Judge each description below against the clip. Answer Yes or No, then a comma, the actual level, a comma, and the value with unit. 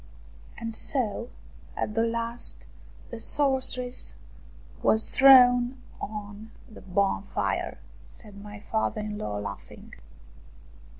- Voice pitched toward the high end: Yes, high, 220 Hz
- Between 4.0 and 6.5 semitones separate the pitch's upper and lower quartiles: No, average, 3.2 semitones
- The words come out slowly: Yes, slow, 110 wpm